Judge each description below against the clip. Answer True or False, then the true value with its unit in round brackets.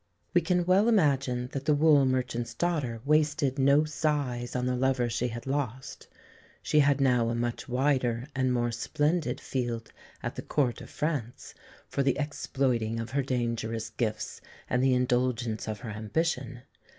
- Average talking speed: True (165 wpm)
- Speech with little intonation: False (3.3 semitones)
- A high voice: False (130 Hz)